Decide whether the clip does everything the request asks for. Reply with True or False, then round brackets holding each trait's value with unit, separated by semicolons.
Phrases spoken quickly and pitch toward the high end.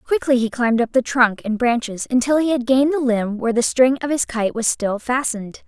True (245 wpm; 245 Hz)